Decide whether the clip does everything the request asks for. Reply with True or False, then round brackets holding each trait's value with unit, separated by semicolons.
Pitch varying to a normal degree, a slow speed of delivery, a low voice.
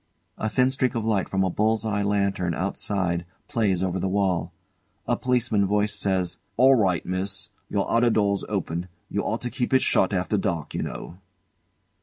False (3.0 semitones; 180 wpm; 100 Hz)